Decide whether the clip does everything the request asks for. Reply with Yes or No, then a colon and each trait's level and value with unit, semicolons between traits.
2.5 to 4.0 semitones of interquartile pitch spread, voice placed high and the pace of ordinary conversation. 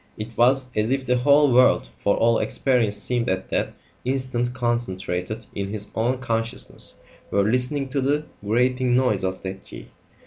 No: average, 3.4 semitones; low, 120 Hz; average, 165 wpm